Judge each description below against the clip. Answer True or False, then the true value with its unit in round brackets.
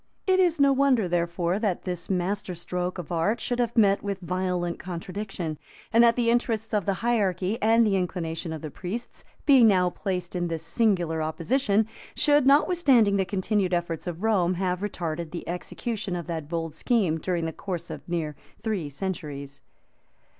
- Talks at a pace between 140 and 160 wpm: False (175 wpm)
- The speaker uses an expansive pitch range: False (4.5 semitones)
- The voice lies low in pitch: False (185 Hz)